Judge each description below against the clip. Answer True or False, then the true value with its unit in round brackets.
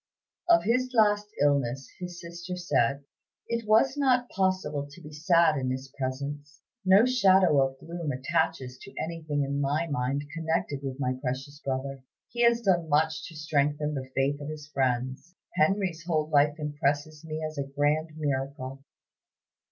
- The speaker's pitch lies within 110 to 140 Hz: False (150 Hz)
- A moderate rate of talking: True (160 wpm)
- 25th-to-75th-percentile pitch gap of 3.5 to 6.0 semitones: True (3.8 semitones)